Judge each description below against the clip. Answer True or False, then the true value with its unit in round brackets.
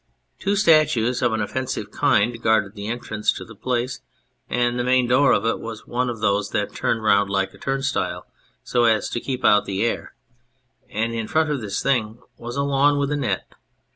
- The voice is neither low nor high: False (120 Hz)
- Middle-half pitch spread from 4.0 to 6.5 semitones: False (3.4 semitones)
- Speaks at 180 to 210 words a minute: True (200 wpm)